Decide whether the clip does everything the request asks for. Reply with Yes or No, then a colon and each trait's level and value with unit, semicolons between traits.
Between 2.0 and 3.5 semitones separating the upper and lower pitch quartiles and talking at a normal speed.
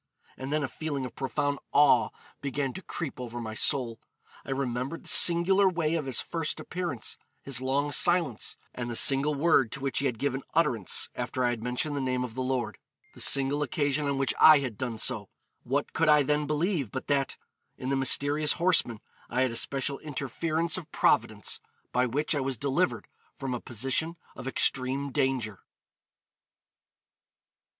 Yes: average, 2.9 semitones; average, 175 wpm